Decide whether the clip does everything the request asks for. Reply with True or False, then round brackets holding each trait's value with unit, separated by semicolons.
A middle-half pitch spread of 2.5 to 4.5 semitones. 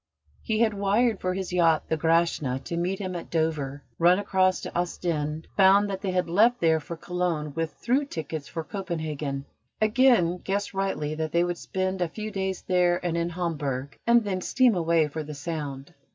True (3.4 semitones)